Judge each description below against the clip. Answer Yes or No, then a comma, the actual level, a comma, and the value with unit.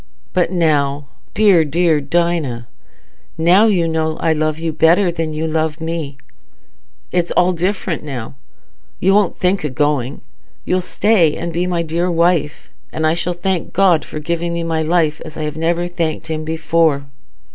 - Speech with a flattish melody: Yes, narrow, 2.1 semitones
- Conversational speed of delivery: Yes, average, 165 wpm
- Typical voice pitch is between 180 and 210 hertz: No, medium, 165 Hz